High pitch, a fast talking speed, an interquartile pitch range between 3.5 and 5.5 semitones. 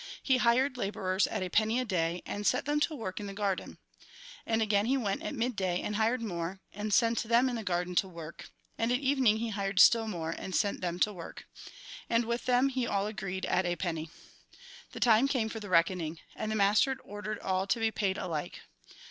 Yes: high, 210 Hz; fast, 220 wpm; average, 3.8 semitones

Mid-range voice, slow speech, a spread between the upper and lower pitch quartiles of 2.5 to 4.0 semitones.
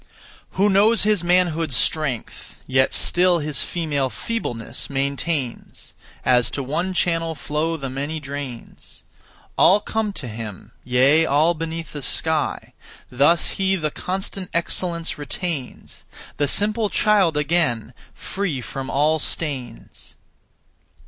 No: medium, 155 Hz; slow, 120 wpm; average, 4.5 semitones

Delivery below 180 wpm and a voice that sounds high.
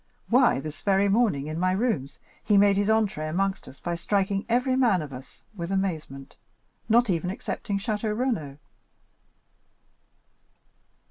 Yes: average, 140 wpm; high, 195 Hz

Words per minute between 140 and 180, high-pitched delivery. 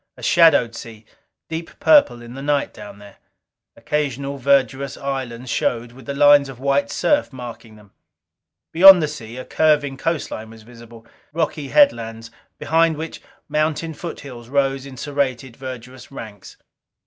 No: average, 145 wpm; low, 135 Hz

